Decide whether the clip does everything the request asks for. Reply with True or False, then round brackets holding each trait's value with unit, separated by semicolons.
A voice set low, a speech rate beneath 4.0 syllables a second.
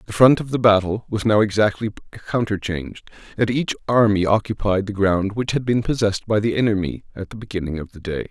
False (105 Hz; 6.0 syllables/s)